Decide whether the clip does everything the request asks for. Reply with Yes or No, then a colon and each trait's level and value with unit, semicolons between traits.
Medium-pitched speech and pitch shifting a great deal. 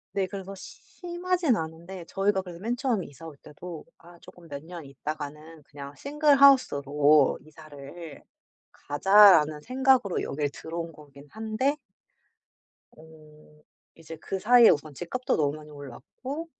Yes: medium, 165 Hz; wide, 6.4 semitones